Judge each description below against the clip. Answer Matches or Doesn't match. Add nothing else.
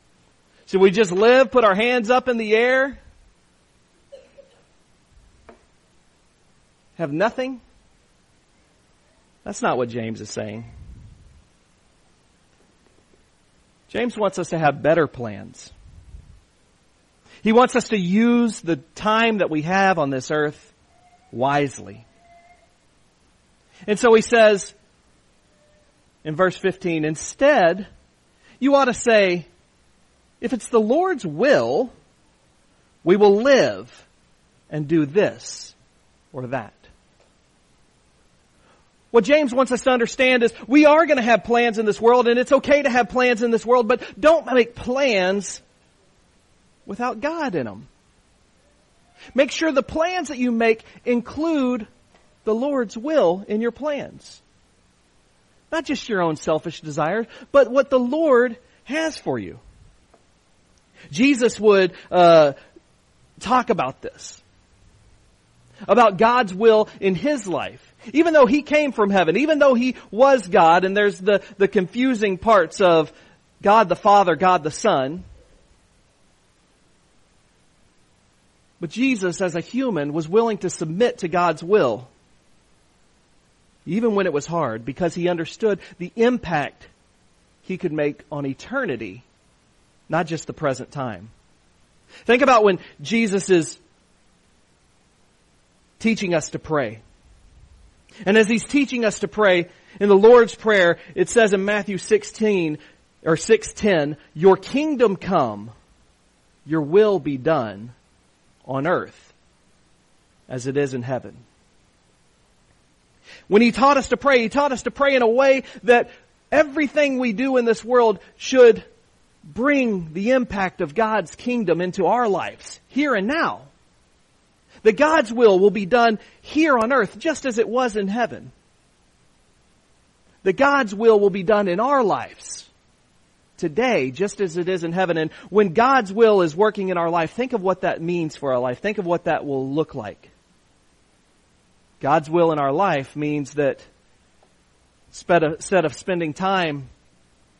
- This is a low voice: Doesn't match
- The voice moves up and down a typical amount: Doesn't match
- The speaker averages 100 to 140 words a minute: Matches